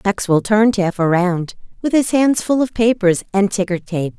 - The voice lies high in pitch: Yes, high, 205 Hz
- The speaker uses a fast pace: No, average, 185 wpm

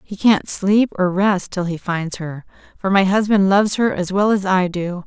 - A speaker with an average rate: No, fast, 225 wpm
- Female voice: Yes, female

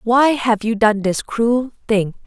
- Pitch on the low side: No, high, 230 Hz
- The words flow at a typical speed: Yes, average, 185 wpm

